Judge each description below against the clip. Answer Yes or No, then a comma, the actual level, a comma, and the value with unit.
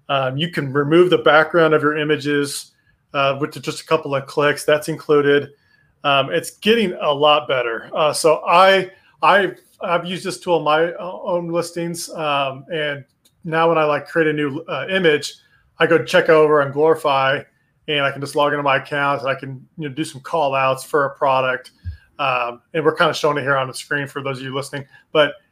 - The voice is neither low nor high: Yes, medium, 150 Hz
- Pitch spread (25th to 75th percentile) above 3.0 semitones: No, average, 2.7 semitones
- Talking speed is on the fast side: Yes, fast, 215 wpm